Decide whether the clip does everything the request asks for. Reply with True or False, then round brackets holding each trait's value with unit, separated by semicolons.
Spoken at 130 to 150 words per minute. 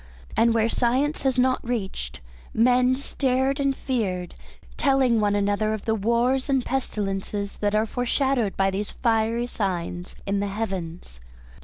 True (145 wpm)